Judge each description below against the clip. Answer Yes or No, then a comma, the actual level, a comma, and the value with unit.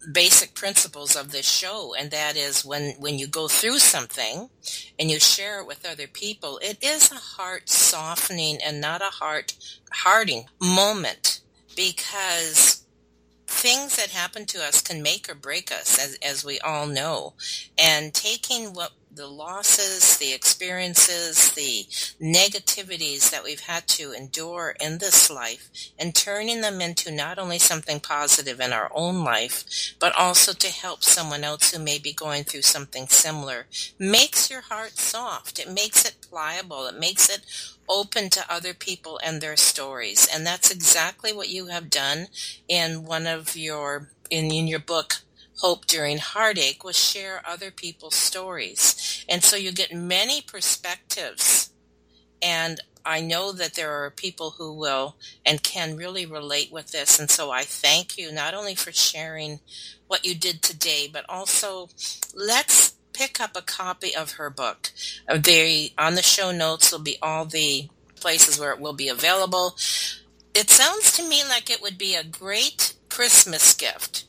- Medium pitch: Yes, medium, 165 Hz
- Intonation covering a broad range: No, average, 4.0 semitones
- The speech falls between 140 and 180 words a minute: Yes, average, 165 wpm